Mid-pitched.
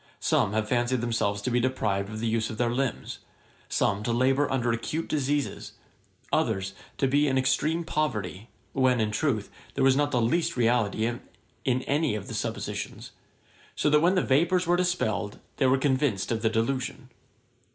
No: low, 125 Hz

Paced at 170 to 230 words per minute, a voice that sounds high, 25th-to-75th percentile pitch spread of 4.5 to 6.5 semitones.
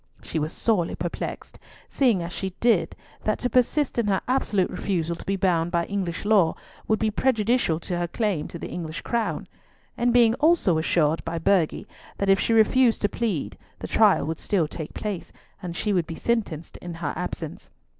Yes: average, 190 wpm; high, 195 Hz; average, 5.0 semitones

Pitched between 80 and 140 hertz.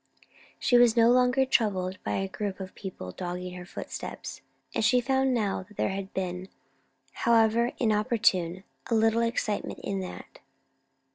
No: high, 210 Hz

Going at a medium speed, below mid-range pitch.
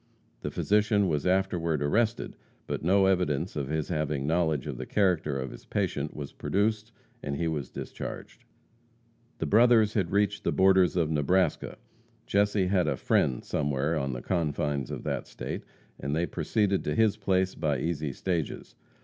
Yes: average, 165 wpm; very low, 85 Hz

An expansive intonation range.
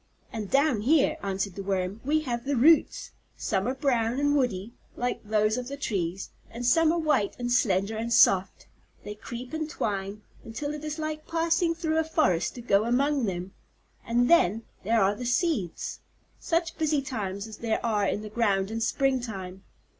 Yes: wide, 6.1 semitones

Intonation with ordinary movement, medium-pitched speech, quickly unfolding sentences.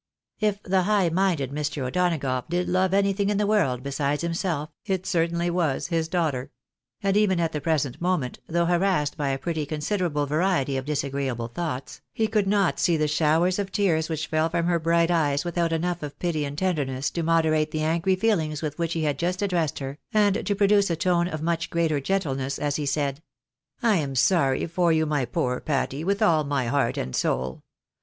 Yes: average, 3.9 semitones; medium, 165 Hz; fast, 210 wpm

